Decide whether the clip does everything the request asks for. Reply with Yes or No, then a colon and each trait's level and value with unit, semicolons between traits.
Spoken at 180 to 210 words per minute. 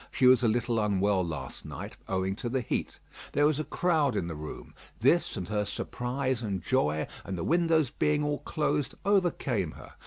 Yes: average, 190 wpm